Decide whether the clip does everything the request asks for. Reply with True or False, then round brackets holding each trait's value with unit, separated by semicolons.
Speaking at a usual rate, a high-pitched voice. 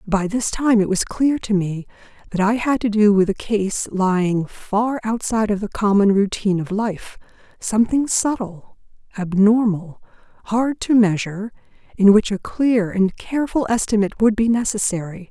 True (160 wpm; 210 Hz)